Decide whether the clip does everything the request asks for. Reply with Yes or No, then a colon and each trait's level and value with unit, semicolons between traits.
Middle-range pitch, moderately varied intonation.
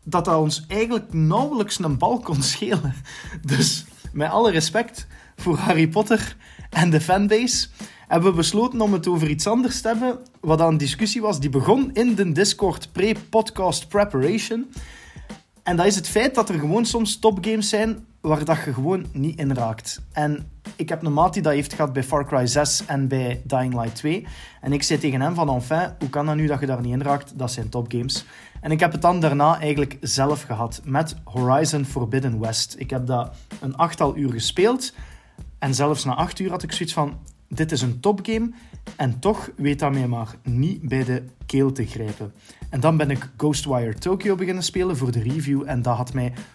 No: medium, 155 Hz; wide, 6.3 semitones